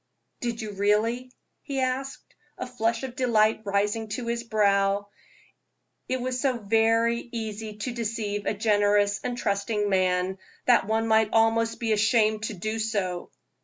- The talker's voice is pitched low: No, high, 220 Hz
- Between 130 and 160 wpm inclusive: Yes, average, 150 wpm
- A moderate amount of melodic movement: No, narrow, 2.3 semitones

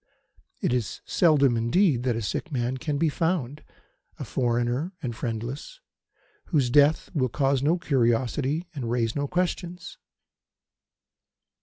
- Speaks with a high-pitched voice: No, low, 135 Hz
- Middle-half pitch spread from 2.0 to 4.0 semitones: No, average, 4.7 semitones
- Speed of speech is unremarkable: No, slow, 130 wpm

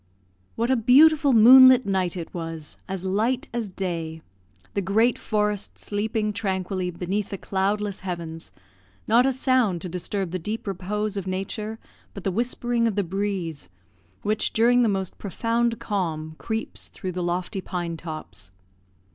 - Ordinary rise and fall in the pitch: Yes, average, 3.9 semitones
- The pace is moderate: Yes, average, 150 wpm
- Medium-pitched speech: No, high, 200 Hz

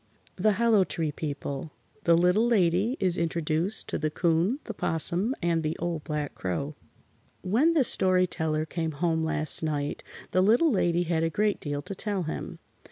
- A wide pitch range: No, average, 3.9 semitones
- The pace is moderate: Yes, average, 170 wpm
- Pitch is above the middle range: No, medium, 170 Hz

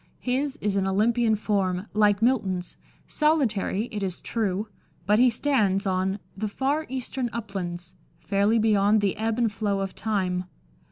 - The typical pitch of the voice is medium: No, high, 210 Hz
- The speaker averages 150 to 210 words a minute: Yes, average, 155 wpm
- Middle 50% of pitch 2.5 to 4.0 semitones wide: Yes, average, 3.2 semitones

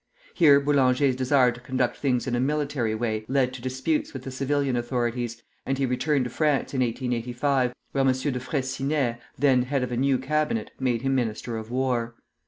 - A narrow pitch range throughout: Yes, narrow, 2.2 semitones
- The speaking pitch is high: No, low, 130 Hz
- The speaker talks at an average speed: Yes, average, 190 wpm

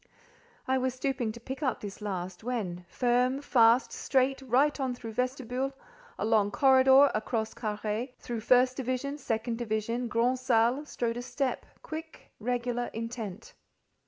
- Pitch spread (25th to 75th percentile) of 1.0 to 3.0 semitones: Yes, average, 2.7 semitones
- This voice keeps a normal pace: No, slow, 125 wpm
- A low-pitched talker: No, high, 245 Hz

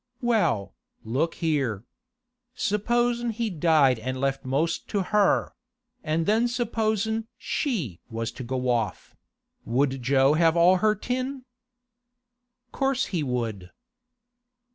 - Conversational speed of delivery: No, slow, 115 wpm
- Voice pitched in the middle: Yes, medium, 165 Hz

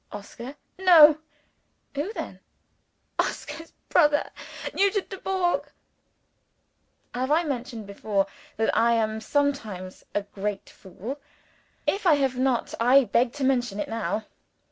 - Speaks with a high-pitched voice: Yes, very high, 255 Hz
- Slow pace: Yes, slow, 120 wpm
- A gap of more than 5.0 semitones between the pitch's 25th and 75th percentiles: Yes, wide, 5.4 semitones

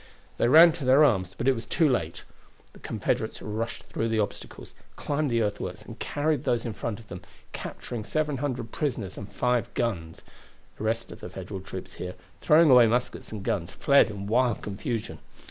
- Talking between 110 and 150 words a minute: No, average, 185 wpm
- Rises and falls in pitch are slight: No, average, 4.2 semitones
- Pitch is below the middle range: Yes, low, 115 Hz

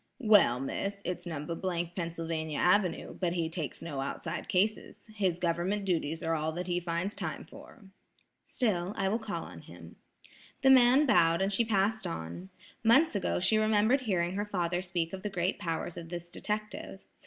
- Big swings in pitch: No, average, 3.8 semitones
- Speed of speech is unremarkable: Yes, average, 175 wpm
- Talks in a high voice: No, medium, 180 Hz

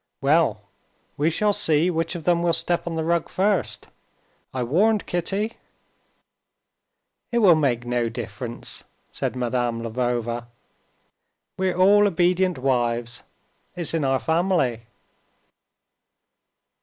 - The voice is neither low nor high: Yes, medium, 160 Hz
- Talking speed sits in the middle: No, slow, 115 wpm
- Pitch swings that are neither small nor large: No, wide, 6.6 semitones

